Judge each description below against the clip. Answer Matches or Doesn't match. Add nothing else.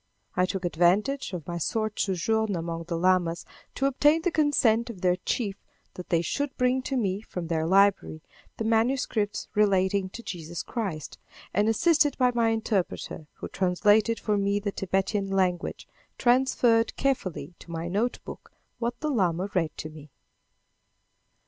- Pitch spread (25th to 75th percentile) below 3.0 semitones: Doesn't match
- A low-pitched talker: Doesn't match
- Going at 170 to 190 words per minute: Doesn't match